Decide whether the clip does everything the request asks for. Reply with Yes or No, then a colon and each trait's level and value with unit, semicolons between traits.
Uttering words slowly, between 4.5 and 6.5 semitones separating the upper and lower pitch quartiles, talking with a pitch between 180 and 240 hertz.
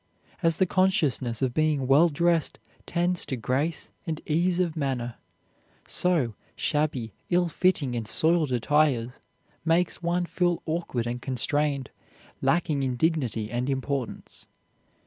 No: slow, 125 wpm; average, 5.1 semitones; medium, 150 Hz